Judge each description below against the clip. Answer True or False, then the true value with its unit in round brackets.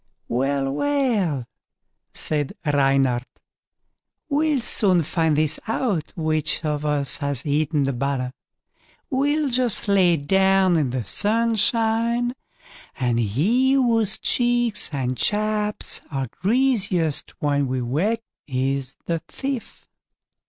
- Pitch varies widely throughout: True (8.6 semitones)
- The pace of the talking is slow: True (110 wpm)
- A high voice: False (165 Hz)